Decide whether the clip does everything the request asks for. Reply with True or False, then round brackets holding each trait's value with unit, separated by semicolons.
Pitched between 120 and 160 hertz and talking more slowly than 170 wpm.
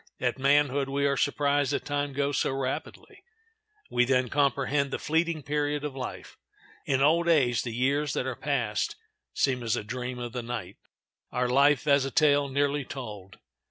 False (140 Hz; 175 wpm)